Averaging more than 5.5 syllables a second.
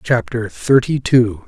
No: 3.7 syllables/s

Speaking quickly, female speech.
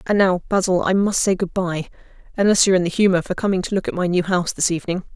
Yes: fast, 255 wpm; female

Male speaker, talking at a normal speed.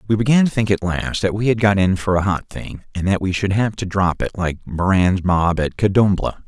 No: male; fast, 260 wpm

